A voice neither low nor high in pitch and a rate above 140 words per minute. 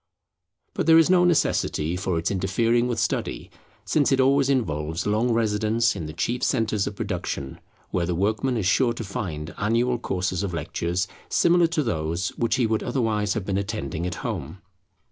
No: low, 105 Hz; average, 180 wpm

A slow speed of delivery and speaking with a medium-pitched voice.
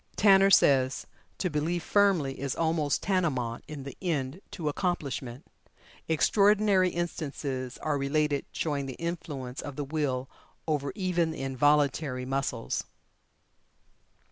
Yes: slow, 115 wpm; medium, 150 Hz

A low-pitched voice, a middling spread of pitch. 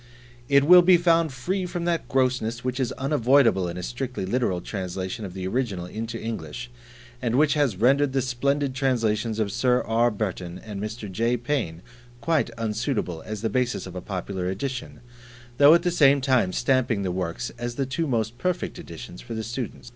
Yes: low, 120 Hz; average, 4.9 semitones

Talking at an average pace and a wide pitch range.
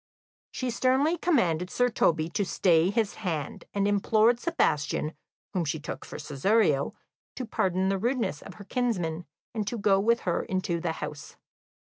Yes: average, 160 wpm; wide, 5.9 semitones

